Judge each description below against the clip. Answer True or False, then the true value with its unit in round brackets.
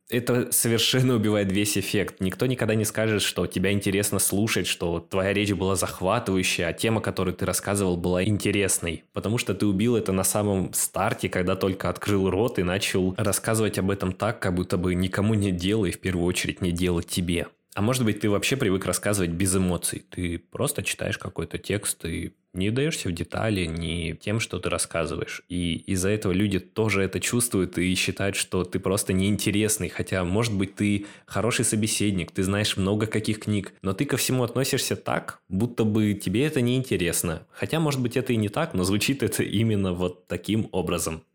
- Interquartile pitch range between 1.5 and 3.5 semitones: True (2.9 semitones)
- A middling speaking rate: False (185 wpm)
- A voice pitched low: True (100 Hz)